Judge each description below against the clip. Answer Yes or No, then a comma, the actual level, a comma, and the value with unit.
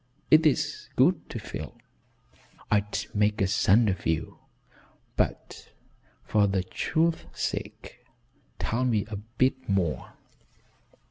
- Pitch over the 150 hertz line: No, low, 105 Hz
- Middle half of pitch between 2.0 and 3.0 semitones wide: No, average, 4.0 semitones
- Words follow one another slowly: Yes, slow, 115 wpm